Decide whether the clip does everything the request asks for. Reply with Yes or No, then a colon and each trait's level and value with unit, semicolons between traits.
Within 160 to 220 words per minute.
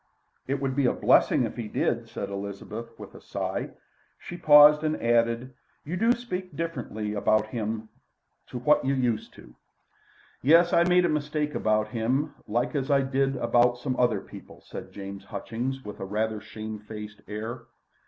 Yes: average, 175 wpm